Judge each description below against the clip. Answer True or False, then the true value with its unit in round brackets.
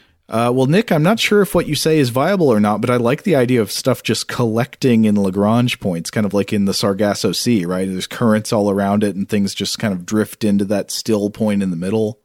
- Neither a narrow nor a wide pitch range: True (3.5 semitones)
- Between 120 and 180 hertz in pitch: False (110 Hz)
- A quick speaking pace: True (255 wpm)